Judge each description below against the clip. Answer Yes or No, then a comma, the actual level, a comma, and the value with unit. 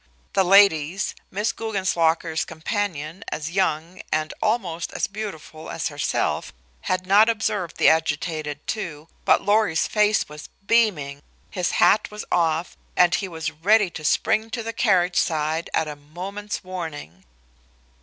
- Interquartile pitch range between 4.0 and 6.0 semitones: Yes, average, 4.6 semitones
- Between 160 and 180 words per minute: No, average, 140 wpm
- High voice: No, medium, 175 Hz